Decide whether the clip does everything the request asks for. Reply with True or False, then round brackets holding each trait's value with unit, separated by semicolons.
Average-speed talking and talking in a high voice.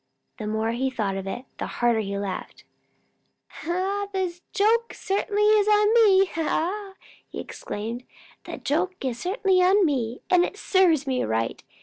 True (145 wpm; 355 Hz)